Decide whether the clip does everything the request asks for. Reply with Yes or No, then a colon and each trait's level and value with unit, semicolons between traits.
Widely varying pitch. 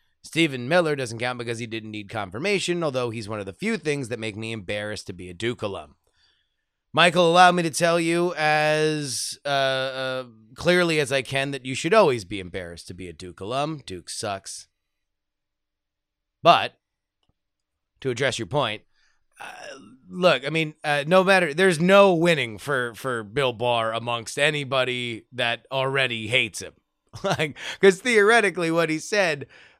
Yes: wide, 6.6 semitones